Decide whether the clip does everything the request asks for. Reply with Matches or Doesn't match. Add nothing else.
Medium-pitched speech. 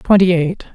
Matches